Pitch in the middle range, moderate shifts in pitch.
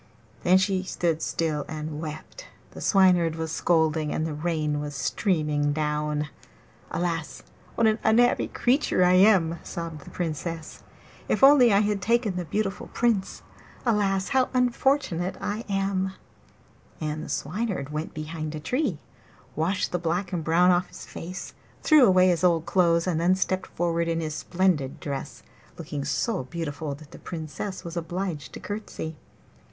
Yes: medium, 170 Hz; average, 3.8 semitones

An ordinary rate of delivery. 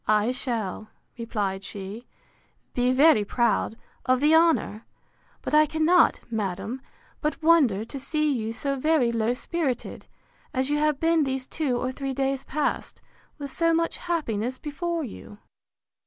Yes: average, 145 wpm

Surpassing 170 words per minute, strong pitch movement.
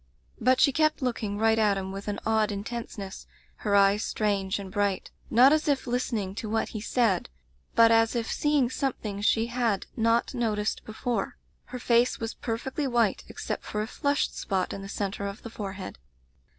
No: average, 185 wpm; average, 3.1 semitones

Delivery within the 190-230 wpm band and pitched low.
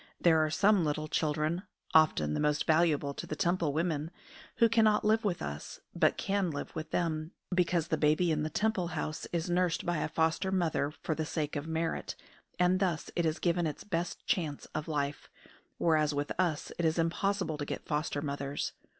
No: average, 195 wpm; medium, 160 Hz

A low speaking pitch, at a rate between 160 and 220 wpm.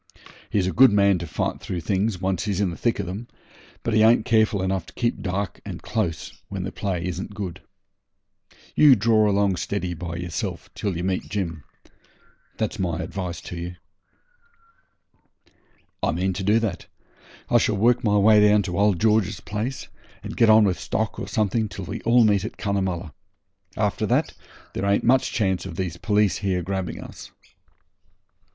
Yes: low, 100 Hz; average, 180 wpm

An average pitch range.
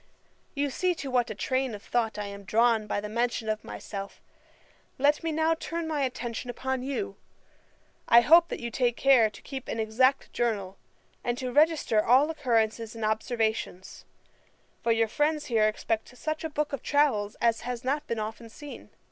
Yes: average, 4.6 semitones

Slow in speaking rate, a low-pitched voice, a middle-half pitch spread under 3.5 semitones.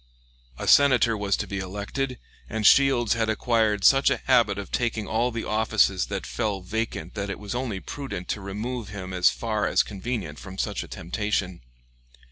No: average, 180 wpm; low, 105 Hz; average, 3.1 semitones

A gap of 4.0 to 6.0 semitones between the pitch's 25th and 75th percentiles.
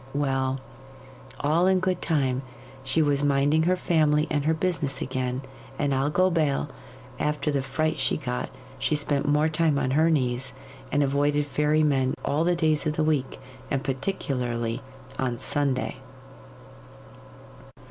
No: average, 2.7 semitones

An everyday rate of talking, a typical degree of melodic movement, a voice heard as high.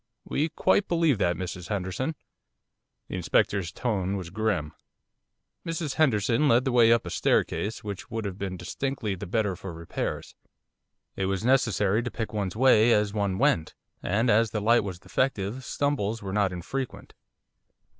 No: average, 160 wpm; average, 4.5 semitones; low, 105 Hz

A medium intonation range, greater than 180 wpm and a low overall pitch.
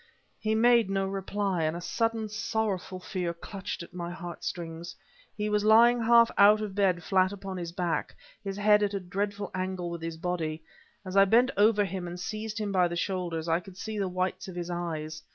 No: average, 3.1 semitones; fast, 205 wpm; high, 190 Hz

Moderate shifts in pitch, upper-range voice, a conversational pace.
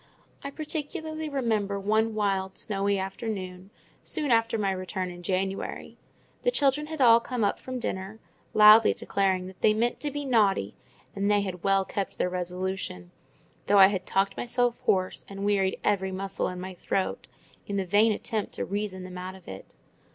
Yes: average, 3.2 semitones; high, 200 Hz; average, 175 wpm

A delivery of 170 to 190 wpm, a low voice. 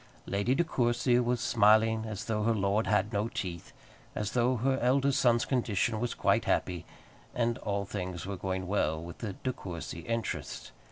Yes: average, 175 wpm; low, 110 Hz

